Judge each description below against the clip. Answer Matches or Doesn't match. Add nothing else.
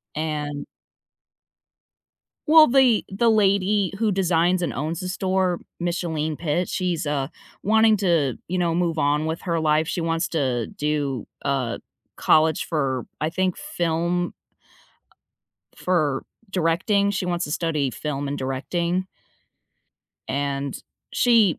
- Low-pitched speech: Doesn't match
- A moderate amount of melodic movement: Matches